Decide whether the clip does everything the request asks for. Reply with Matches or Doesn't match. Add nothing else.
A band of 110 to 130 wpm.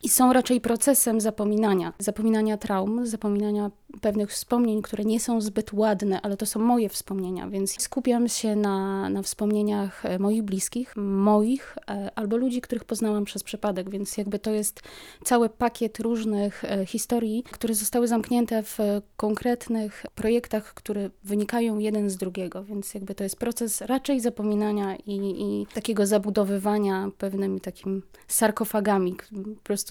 Doesn't match